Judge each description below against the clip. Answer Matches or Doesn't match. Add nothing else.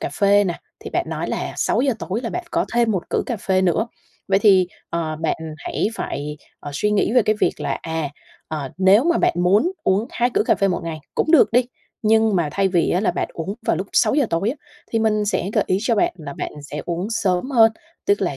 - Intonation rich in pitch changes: Doesn't match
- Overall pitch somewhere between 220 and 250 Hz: Doesn't match